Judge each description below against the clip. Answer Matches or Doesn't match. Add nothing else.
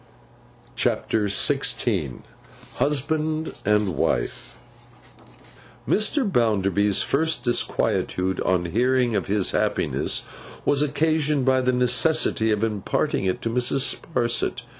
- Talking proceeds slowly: Matches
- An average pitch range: Doesn't match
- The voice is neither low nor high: Doesn't match